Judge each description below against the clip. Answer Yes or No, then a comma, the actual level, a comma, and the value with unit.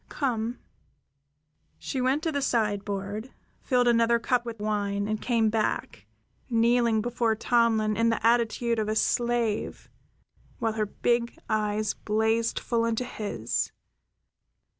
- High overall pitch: Yes, high, 230 Hz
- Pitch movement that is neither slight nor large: No, narrow, 1.8 semitones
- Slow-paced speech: Yes, slow, 125 wpm